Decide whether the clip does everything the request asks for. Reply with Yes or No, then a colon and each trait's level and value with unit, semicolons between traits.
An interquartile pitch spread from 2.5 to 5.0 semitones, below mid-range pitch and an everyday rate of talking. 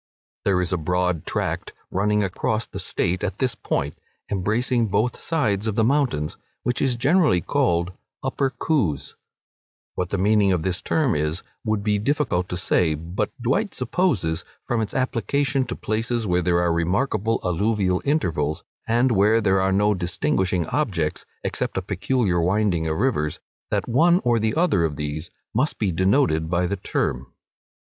No: wide, 5.4 semitones; low, 100 Hz; average, 165 wpm